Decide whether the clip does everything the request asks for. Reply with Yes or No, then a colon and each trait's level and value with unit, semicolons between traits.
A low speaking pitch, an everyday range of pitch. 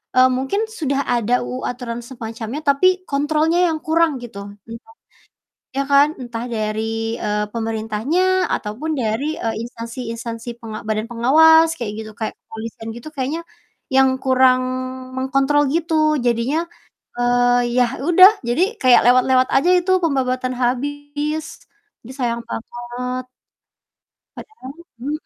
No: very high, 255 Hz; average, 3.9 semitones